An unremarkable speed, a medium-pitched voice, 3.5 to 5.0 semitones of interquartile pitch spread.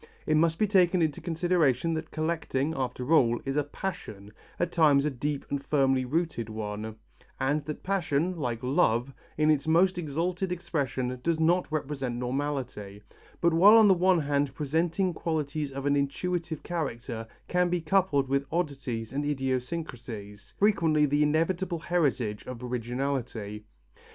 Yes: average, 150 wpm; medium, 145 Hz; average, 4.6 semitones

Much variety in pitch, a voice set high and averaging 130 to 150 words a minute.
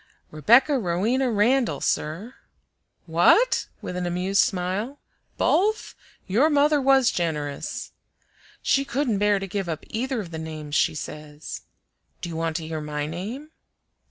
Yes: wide, 8.3 semitones; high, 195 Hz; average, 140 wpm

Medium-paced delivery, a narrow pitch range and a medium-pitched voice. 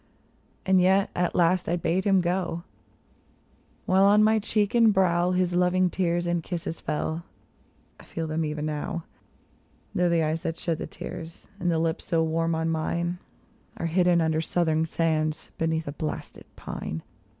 Yes: average, 165 wpm; narrow, 2.0 semitones; medium, 170 Hz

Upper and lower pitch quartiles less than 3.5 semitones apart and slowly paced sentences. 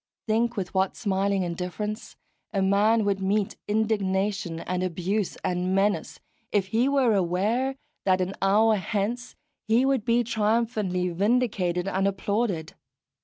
Yes: average, 2.8 semitones; slow, 130 wpm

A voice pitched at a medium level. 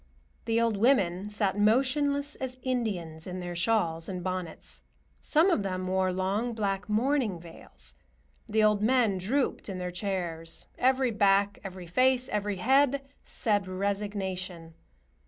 No: high, 200 Hz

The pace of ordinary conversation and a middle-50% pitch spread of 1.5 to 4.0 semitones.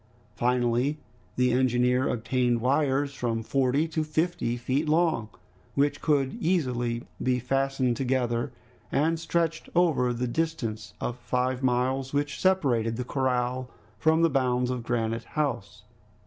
No: slow, 130 wpm; average, 3.1 semitones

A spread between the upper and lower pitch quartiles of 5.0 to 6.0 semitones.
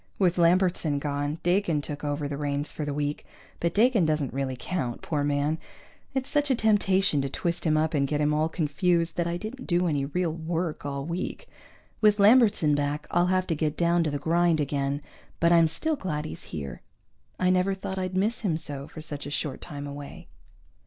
No: average, 3.9 semitones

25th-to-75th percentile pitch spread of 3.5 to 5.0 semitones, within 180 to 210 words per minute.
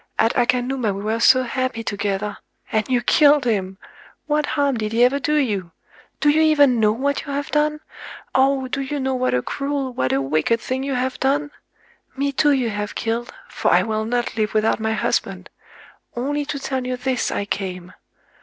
Yes: average, 4.4 semitones; average, 185 wpm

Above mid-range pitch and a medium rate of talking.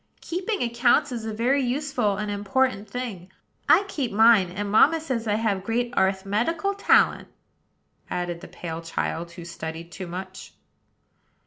Yes: high, 215 Hz; average, 160 wpm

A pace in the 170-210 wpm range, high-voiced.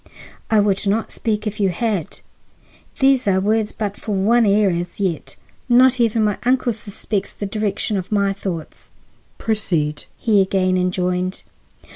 No: average, 150 wpm; high, 205 Hz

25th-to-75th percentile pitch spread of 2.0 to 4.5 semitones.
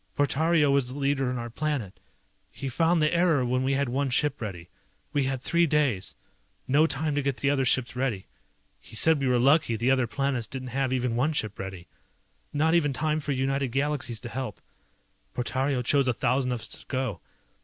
Yes: average, 2.7 semitones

